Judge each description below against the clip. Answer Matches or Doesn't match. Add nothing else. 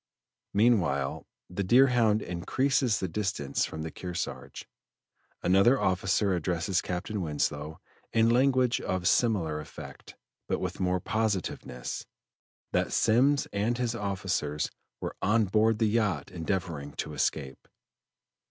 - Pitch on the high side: Doesn't match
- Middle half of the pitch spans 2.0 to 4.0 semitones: Doesn't match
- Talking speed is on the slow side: Matches